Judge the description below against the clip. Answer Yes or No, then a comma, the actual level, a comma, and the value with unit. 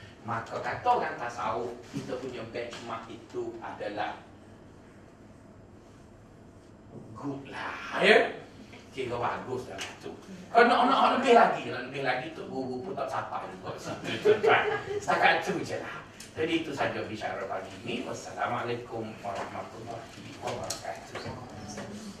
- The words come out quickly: No, average, 120 wpm